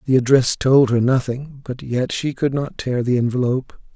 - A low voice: Yes, low, 130 Hz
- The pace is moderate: Yes, average, 195 wpm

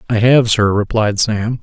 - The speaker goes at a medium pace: Yes, average, 185 wpm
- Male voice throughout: Yes, male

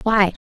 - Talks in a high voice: Yes, high, 205 Hz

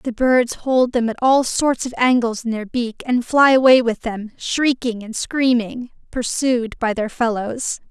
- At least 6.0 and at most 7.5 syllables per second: No, 4.0 syllables/s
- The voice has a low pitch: No, high, 240 Hz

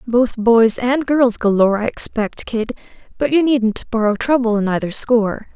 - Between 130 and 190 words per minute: Yes, average, 175 wpm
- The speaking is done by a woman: Yes, female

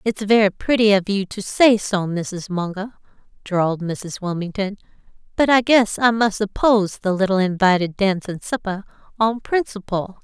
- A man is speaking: No, female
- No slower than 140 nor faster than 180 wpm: Yes, average, 160 wpm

